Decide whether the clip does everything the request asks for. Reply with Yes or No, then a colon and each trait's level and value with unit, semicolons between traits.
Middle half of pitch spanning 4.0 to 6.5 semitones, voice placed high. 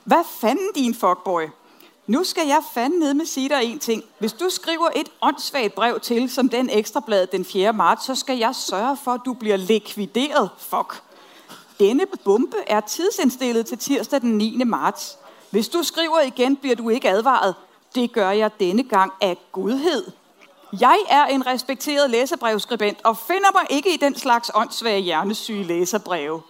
Yes: wide, 5.4 semitones; high, 245 Hz